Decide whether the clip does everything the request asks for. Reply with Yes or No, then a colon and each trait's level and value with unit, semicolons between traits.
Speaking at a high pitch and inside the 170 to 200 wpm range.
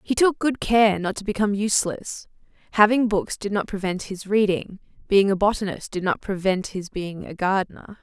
Yes: high, 200 Hz; average, 185 wpm